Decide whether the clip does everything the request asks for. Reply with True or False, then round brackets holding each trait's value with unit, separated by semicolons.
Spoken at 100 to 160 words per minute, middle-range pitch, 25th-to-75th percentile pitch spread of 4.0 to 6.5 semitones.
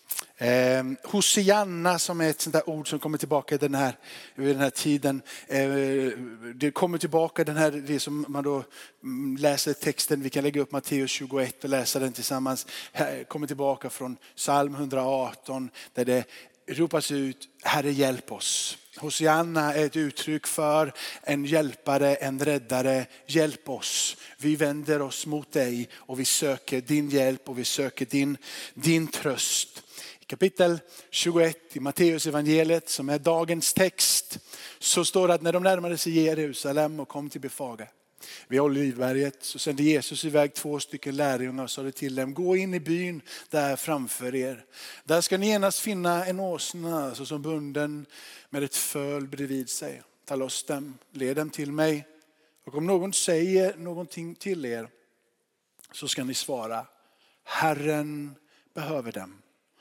False (155 wpm; 145 Hz; 2.9 semitones)